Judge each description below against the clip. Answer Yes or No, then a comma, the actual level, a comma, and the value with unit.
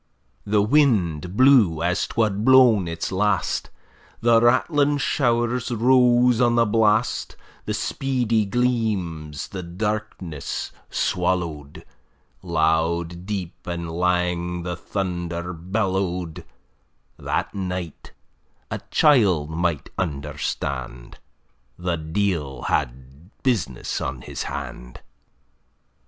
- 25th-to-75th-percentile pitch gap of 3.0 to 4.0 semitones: No, wide, 5.4 semitones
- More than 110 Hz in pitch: No, very low, 90 Hz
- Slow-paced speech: Yes, slow, 95 wpm